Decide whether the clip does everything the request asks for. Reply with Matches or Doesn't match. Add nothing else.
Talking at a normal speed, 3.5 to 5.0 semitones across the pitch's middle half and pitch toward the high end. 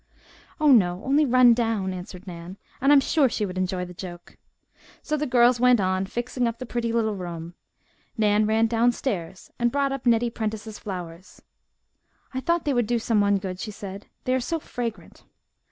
Matches